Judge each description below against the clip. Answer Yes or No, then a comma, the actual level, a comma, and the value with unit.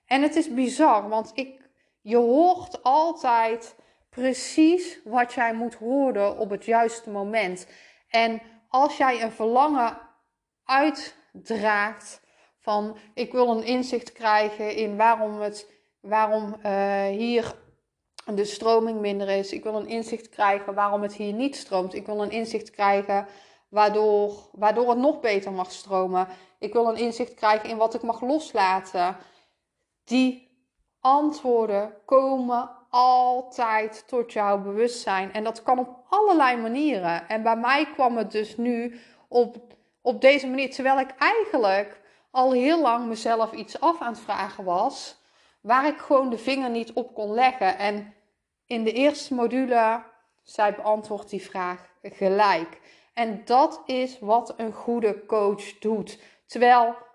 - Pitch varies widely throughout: No, average, 3.4 semitones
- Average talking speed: Yes, average, 145 wpm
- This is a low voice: No, high, 230 Hz